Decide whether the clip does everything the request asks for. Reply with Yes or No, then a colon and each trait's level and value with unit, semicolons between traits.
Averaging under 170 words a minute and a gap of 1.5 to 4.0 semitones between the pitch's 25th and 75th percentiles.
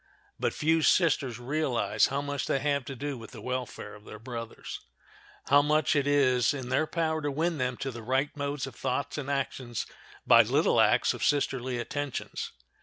No: average, 180 wpm; average, 2.8 semitones